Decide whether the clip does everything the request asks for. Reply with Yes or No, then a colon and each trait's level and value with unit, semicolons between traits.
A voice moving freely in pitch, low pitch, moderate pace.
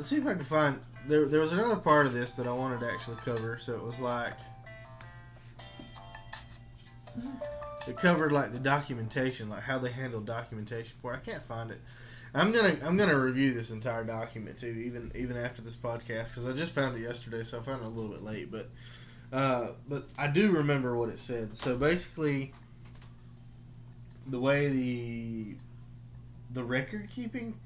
No: narrow, 2.4 semitones; low, 120 Hz; average, 180 wpm